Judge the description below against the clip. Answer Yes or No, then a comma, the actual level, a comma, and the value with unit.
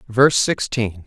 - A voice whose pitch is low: Yes, low, 115 Hz